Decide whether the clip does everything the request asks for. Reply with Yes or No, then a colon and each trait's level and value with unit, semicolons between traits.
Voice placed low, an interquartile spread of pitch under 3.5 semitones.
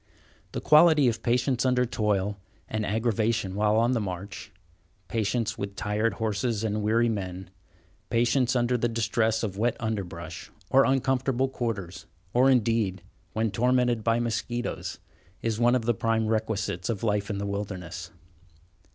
Yes: low, 110 Hz; average, 3.0 semitones